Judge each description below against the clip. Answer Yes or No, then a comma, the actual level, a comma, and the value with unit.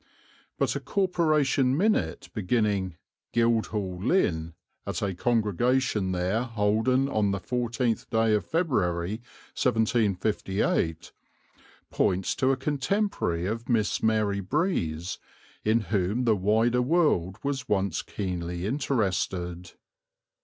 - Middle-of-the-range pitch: No, low, 110 Hz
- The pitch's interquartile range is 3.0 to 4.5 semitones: No, average, 5.2 semitones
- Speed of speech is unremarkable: No, slow, 105 wpm